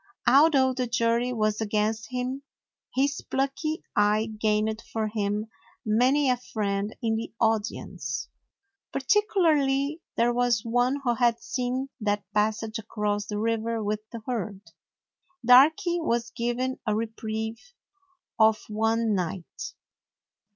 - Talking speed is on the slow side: Yes, slow, 125 wpm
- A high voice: Yes, high, 230 Hz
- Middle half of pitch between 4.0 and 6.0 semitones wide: No, average, 3.2 semitones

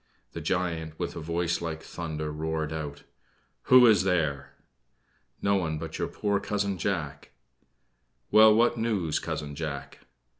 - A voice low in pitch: Yes, very low, 85 Hz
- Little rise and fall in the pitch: No, average, 4.2 semitones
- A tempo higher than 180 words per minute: No, average, 140 wpm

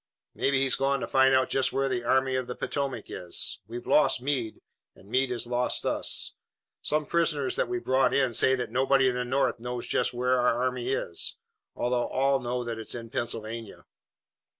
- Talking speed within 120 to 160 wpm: No, average, 195 wpm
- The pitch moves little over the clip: Yes, narrow, 1.9 semitones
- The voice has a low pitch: Yes, low, 130 Hz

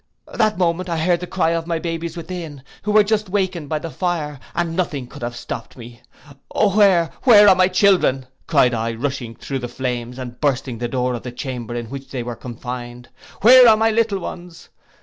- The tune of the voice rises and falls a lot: Yes, wide, 6.8 semitones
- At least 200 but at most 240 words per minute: Yes, fast, 205 wpm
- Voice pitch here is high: No, medium, 160 Hz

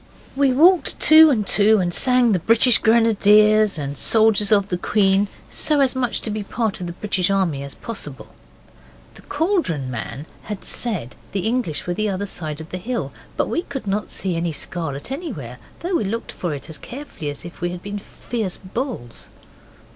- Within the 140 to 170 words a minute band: No, average, 190 wpm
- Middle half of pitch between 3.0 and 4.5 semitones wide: No, wide, 5.4 semitones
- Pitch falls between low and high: No, high, 205 Hz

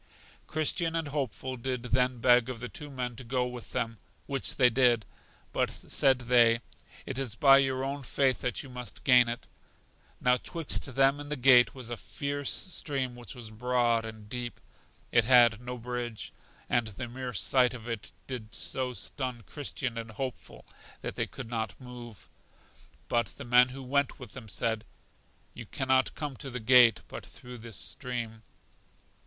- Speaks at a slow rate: No, average, 175 wpm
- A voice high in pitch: No, low, 125 Hz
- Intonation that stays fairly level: Yes, narrow, 2.1 semitones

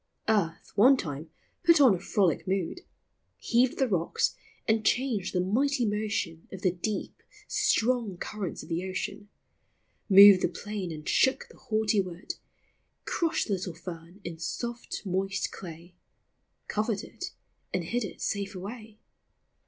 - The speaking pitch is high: Yes, high, 200 Hz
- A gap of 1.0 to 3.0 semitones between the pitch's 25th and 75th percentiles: No, average, 4.0 semitones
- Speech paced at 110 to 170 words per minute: Yes, average, 145 wpm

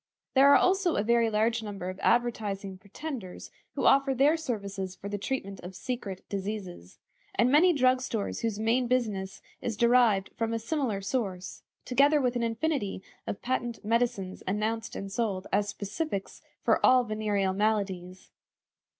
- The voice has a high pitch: Yes, high, 220 Hz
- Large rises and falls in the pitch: No, average, 4.2 semitones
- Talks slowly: No, average, 155 wpm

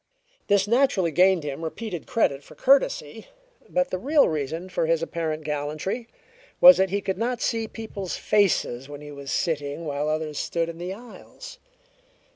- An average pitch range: No, wide, 5.8 semitones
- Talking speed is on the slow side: No, average, 165 wpm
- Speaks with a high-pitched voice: No, medium, 175 Hz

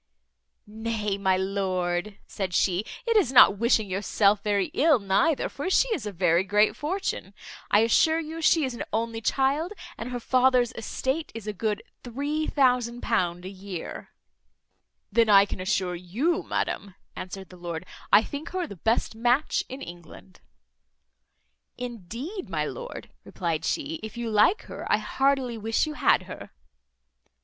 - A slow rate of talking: No, average, 155 wpm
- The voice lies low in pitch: No, high, 225 Hz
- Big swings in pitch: Yes, wide, 5.9 semitones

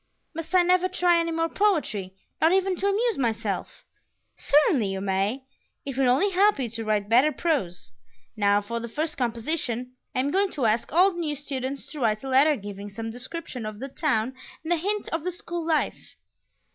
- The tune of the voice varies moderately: No, wide, 6.9 semitones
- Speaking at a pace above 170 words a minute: Yes, average, 195 wpm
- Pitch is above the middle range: Yes, very high, 275 Hz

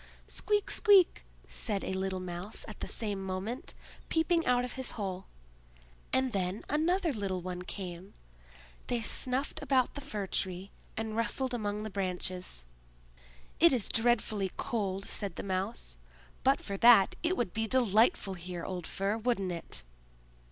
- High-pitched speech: Yes, high, 205 Hz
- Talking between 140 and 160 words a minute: Yes, average, 150 wpm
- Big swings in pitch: No, average, 4.8 semitones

